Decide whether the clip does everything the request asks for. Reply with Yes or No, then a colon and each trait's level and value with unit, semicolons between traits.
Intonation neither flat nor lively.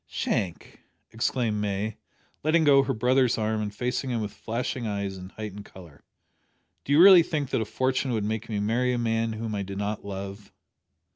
Yes: average, 3.7 semitones